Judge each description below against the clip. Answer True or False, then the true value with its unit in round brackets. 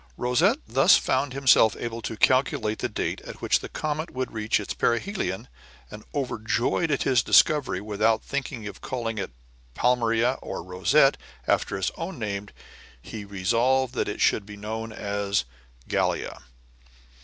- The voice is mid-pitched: False (115 Hz)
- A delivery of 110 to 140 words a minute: False (150 wpm)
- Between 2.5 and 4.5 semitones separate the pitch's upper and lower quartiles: True (4.1 semitones)